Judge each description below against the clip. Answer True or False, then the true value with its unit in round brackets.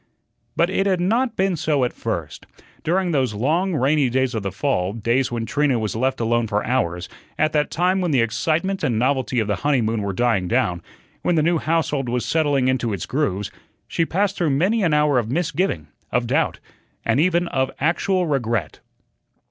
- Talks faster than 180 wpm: True (190 wpm)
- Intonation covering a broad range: True (6.6 semitones)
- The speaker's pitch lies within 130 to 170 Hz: True (135 Hz)